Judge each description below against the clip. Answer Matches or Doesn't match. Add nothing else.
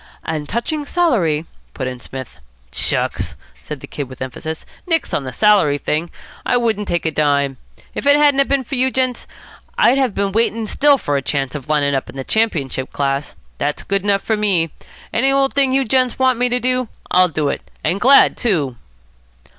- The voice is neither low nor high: Doesn't match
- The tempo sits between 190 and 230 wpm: Matches